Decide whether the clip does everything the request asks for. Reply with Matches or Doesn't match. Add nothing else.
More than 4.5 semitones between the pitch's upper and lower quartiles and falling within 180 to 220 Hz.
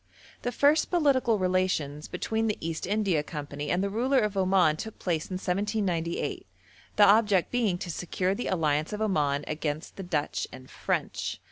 Matches